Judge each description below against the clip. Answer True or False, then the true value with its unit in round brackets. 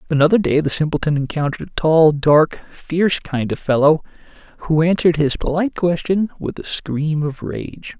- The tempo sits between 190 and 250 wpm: False (165 wpm)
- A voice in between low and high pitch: True (160 Hz)